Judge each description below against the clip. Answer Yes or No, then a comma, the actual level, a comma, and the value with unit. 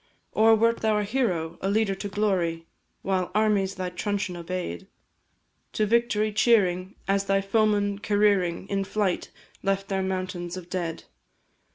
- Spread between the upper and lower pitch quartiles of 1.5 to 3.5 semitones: Yes, narrow, 2.4 semitones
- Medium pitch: No, high, 195 Hz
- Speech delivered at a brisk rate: No, average, 145 wpm